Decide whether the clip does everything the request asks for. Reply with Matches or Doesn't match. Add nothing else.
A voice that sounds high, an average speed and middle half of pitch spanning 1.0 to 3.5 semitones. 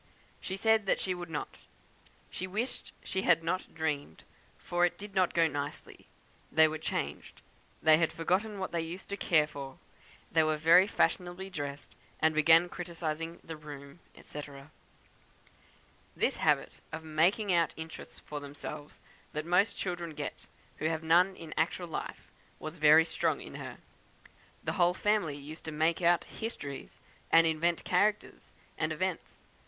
Doesn't match